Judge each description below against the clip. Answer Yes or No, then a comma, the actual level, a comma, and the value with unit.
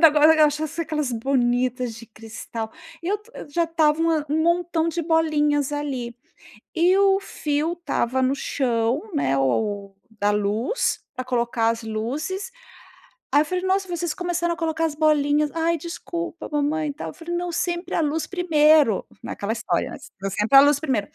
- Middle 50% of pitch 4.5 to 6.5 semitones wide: Yes, average, 5.0 semitones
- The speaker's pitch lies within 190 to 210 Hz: No, very high, 300 Hz